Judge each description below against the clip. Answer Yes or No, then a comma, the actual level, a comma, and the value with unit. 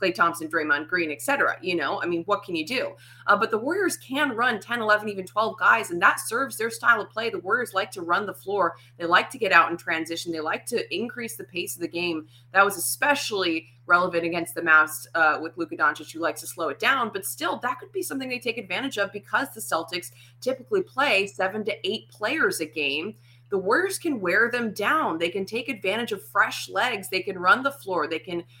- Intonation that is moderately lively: No, wide, 6.6 semitones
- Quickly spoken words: Yes, fast, 235 wpm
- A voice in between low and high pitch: No, high, 195 Hz